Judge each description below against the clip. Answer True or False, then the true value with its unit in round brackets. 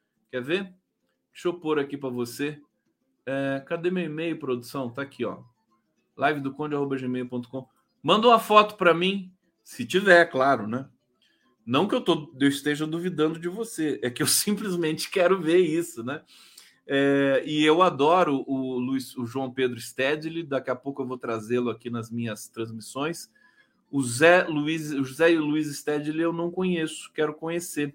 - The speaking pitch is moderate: True (150 Hz)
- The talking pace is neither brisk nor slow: True (170 wpm)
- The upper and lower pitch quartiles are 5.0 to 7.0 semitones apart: False (4.4 semitones)